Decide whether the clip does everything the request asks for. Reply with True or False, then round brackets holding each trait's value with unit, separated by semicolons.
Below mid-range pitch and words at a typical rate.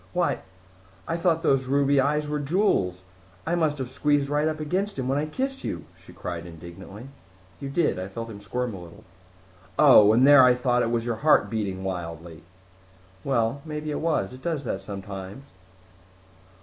True (130 Hz; 180 wpm)